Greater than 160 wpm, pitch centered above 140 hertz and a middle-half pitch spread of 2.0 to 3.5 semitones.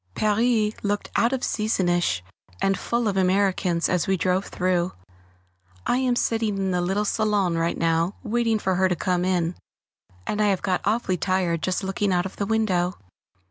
Yes: average, 175 wpm; high, 190 Hz; average, 2.9 semitones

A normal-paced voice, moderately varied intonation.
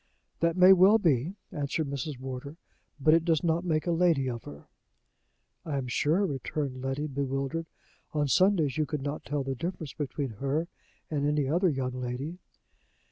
Yes: average, 170 wpm; average, 3.7 semitones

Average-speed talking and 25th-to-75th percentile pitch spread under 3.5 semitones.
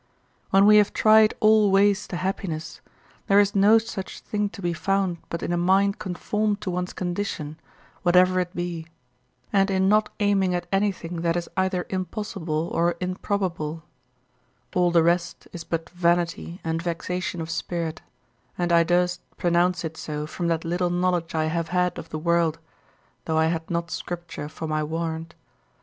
Yes: average, 170 wpm; narrow, 2.5 semitones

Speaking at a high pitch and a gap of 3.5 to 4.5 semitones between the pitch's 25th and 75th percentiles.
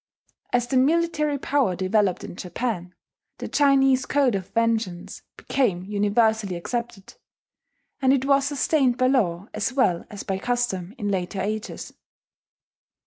No: high, 230 Hz; wide, 5.5 semitones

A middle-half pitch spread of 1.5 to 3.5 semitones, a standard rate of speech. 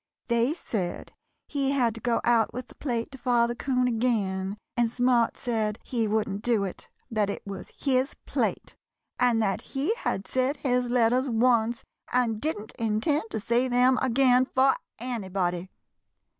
Yes: average, 2.7 semitones; average, 155 wpm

